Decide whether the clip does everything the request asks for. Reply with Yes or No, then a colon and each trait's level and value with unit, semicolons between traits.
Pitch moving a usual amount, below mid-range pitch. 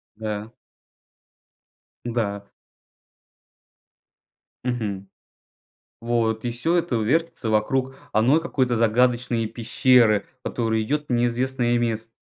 No: narrow, 2.3 semitones; low, 120 Hz